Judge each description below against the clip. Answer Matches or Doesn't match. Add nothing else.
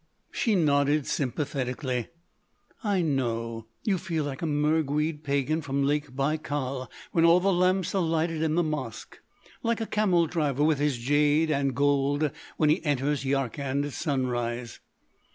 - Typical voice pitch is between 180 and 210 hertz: Doesn't match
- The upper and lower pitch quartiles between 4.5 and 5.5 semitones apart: Doesn't match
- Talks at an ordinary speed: Matches